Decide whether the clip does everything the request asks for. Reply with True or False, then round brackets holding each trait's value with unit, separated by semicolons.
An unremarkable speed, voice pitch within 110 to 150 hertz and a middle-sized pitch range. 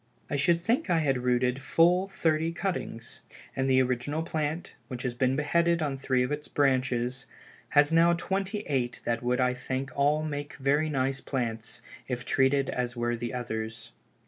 True (170 wpm; 135 Hz; 3.9 semitones)